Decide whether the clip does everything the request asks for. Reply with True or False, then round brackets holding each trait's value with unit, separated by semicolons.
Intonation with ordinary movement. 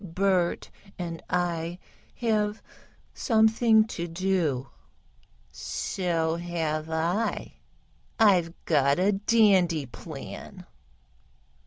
True (4.1 semitones)